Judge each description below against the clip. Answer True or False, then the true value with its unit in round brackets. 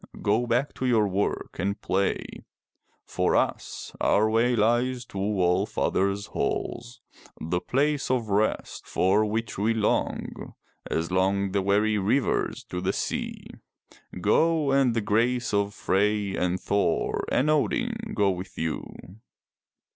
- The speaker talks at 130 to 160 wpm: True (140 wpm)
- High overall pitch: False (105 Hz)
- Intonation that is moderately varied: True (3.8 semitones)